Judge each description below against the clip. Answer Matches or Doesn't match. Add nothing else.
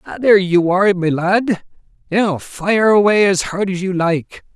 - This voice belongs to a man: Matches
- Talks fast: Doesn't match